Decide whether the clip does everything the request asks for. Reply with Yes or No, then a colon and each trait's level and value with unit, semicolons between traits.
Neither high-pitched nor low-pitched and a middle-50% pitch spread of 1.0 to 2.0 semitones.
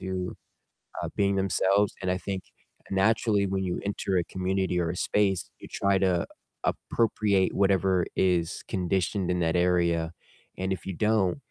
No: very low, 95 Hz; narrow, 1.7 semitones